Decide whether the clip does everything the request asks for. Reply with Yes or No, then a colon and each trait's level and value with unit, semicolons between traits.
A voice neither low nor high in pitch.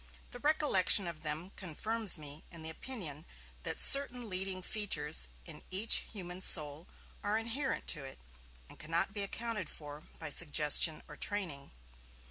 Yes: medium, 180 Hz